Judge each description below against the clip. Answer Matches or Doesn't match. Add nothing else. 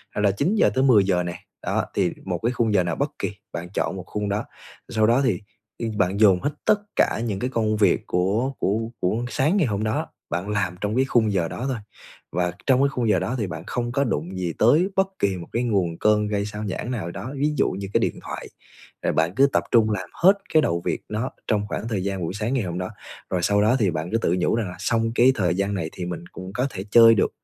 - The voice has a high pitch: Doesn't match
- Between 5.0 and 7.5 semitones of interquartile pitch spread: Doesn't match